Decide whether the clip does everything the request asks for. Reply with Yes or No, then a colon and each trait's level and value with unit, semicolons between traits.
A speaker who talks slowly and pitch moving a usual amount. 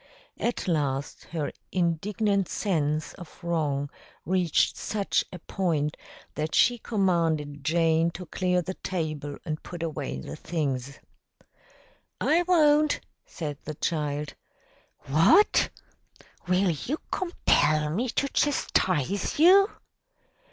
Yes: slow, 110 wpm; average, 4.7 semitones